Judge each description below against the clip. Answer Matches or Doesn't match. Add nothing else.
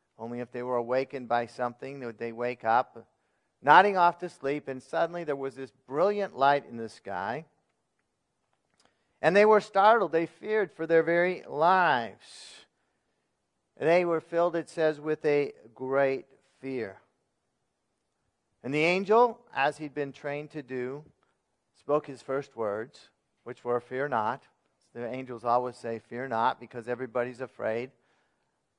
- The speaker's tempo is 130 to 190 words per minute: Matches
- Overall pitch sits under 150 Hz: Matches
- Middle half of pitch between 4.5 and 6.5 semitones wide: Matches